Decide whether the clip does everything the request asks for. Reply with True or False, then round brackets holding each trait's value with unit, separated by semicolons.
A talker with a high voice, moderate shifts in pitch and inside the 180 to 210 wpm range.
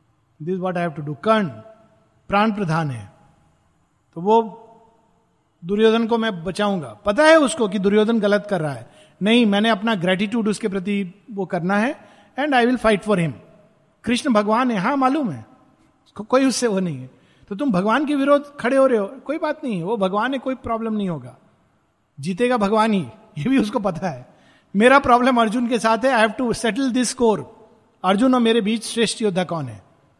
True (215 Hz; 4.2 semitones; 190 wpm)